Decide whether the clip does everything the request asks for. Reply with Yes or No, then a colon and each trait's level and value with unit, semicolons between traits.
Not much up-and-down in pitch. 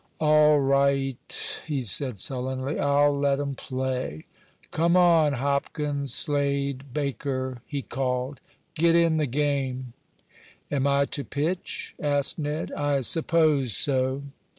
Yes: narrow, 2.0 semitones